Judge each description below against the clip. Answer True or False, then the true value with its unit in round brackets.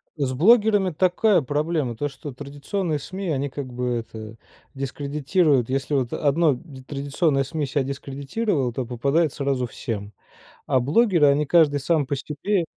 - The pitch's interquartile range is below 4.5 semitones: True (3.7 semitones)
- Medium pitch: True (145 Hz)